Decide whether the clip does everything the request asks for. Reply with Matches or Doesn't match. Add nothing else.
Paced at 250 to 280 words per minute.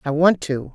Doesn't match